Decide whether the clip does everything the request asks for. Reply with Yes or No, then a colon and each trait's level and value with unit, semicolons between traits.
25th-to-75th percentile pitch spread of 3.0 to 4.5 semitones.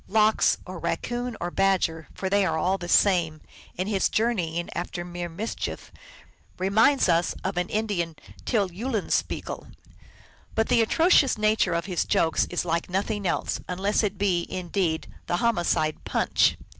Yes: average, 3.6 semitones